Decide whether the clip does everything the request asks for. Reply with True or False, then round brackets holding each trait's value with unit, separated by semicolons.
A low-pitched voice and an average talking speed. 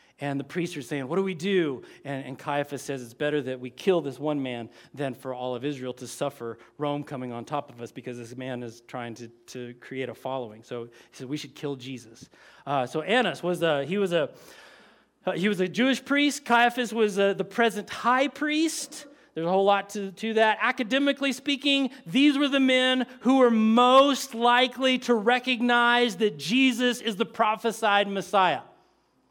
False (190 Hz; 195 wpm)